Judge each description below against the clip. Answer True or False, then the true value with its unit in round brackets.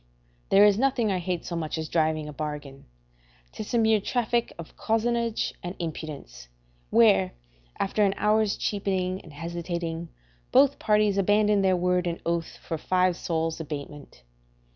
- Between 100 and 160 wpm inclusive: True (150 wpm)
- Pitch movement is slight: False (4.6 semitones)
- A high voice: False (180 Hz)